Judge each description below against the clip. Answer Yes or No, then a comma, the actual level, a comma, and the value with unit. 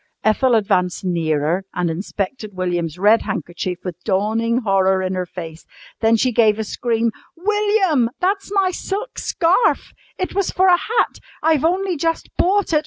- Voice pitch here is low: No, high, 225 Hz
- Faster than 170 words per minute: No, average, 160 wpm